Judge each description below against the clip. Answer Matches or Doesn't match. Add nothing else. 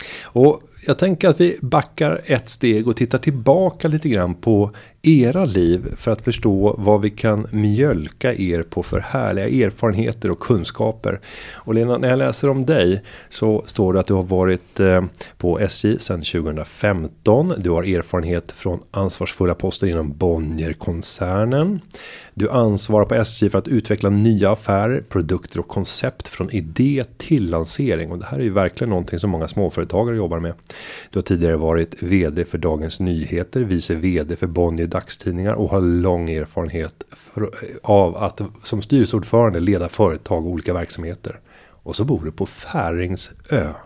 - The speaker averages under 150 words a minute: Doesn't match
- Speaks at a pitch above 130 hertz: Doesn't match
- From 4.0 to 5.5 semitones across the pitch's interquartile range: Matches